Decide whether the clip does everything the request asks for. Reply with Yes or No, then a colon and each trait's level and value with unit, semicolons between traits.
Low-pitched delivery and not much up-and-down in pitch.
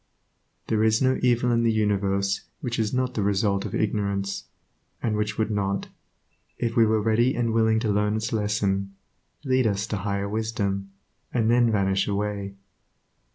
Yes: low, 105 Hz; narrow, 2.3 semitones